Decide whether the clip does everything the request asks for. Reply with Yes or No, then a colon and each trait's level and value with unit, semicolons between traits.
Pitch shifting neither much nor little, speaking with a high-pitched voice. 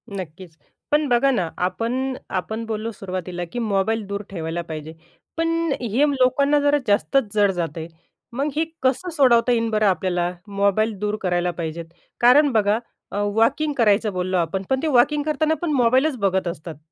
No: wide, 6.1 semitones; high, 215 Hz